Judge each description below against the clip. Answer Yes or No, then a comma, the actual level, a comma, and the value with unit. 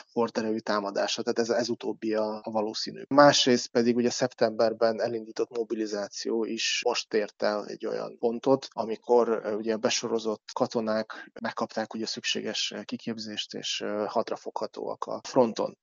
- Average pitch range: No, narrow, 1.5 semitones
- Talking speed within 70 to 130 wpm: Yes, average, 125 wpm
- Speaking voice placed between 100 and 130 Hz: Yes, low, 115 Hz